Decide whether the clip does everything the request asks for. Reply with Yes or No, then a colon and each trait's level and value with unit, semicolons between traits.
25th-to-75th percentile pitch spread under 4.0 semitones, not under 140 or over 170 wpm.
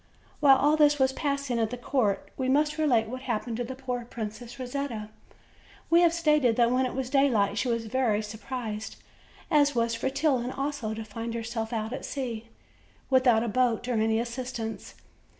No: average, 3.2 semitones; average, 185 wpm